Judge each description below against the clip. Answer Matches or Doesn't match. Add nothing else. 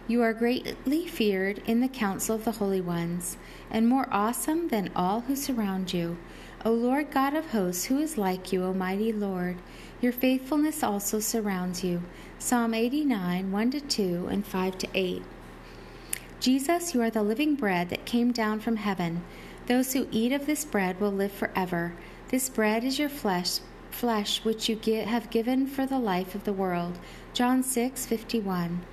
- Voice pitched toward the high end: Matches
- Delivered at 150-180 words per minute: Matches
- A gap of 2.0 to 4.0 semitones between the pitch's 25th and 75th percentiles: Doesn't match